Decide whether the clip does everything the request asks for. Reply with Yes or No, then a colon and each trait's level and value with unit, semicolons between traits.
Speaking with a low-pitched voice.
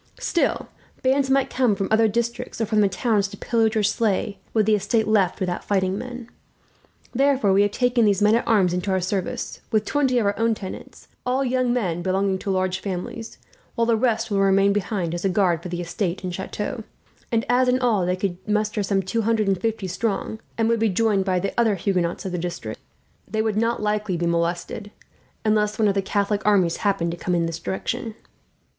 No: high, 205 Hz